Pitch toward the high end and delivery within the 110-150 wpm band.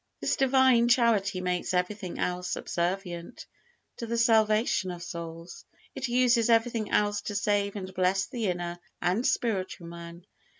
Yes: high, 195 Hz; average, 140 wpm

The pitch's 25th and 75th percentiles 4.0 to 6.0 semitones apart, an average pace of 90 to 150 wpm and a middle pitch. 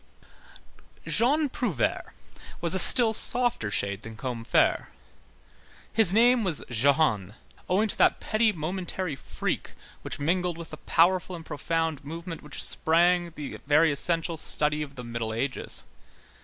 Yes: average, 4.9 semitones; slow, 135 wpm; medium, 165 Hz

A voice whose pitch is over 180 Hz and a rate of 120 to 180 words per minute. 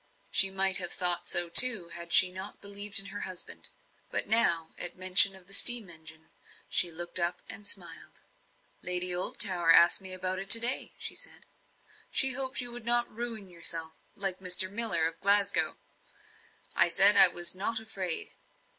Yes: high, 190 Hz; average, 170 wpm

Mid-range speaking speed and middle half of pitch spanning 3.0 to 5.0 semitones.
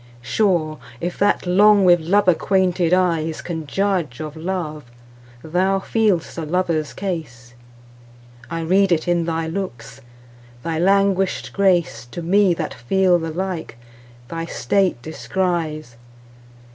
No: slow, 115 wpm; average, 3.5 semitones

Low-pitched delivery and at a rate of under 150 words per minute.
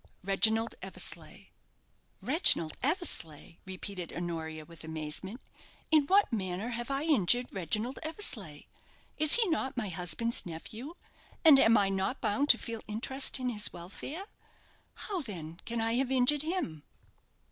No: high, 225 Hz; slow, 135 wpm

